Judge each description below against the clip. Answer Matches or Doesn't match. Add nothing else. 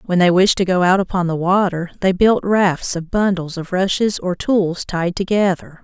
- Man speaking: Doesn't match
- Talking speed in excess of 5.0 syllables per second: Doesn't match